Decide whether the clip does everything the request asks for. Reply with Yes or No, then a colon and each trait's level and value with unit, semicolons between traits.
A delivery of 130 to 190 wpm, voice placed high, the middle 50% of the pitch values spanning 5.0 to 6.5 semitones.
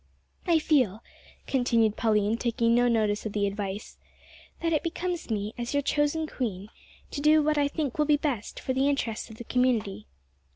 Yes: average, 180 wpm; high, 245 Hz; wide, 5.4 semitones